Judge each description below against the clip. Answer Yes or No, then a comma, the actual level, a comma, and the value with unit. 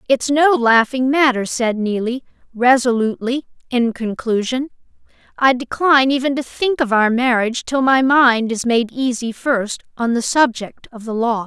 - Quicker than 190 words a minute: No, average, 155 wpm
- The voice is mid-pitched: No, high, 245 Hz